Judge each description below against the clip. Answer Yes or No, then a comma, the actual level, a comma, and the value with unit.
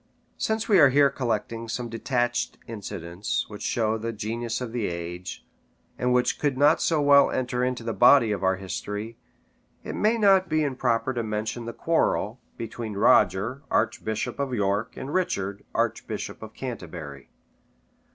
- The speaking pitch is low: Yes, low, 115 Hz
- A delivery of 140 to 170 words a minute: Yes, average, 160 wpm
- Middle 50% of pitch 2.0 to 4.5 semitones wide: Yes, average, 4.1 semitones